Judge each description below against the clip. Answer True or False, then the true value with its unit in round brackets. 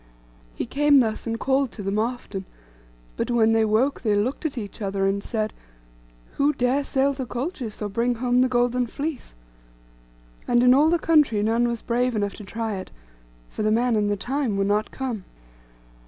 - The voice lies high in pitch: True (235 Hz)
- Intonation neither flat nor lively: True (3.7 semitones)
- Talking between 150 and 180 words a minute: False (190 wpm)